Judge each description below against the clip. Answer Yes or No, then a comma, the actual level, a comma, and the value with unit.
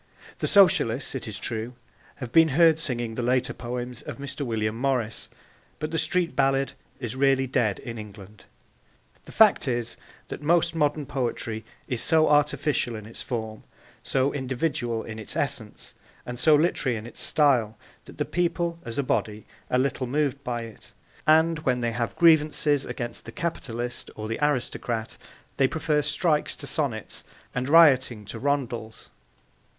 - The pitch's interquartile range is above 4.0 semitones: Yes, average, 4.4 semitones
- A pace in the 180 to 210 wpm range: No, average, 160 wpm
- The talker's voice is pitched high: No, low, 130 Hz